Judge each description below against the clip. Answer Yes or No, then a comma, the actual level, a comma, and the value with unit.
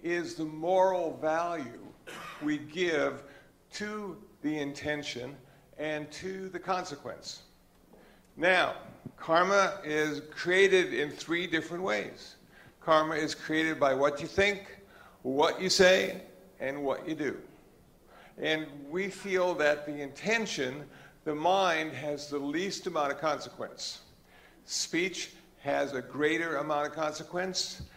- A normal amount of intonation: Yes, average, 3.7 semitones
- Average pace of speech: No, slow, 120 wpm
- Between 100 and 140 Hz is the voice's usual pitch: No, medium, 155 Hz